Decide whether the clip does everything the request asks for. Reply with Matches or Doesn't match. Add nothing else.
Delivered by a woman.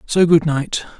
Doesn't match